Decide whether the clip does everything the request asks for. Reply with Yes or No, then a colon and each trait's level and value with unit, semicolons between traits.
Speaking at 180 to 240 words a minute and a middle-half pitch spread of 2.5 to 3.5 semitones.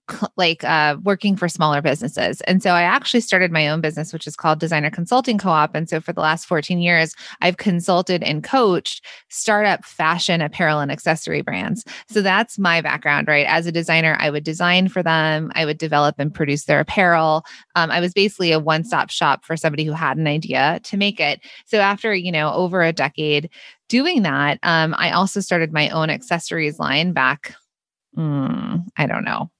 Yes: average, 195 wpm; average, 2.9 semitones